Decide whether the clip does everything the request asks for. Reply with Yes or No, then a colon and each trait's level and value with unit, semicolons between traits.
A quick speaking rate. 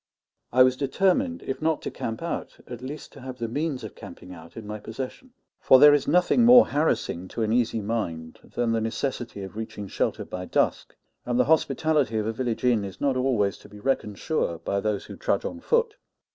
Yes: fast, 215 wpm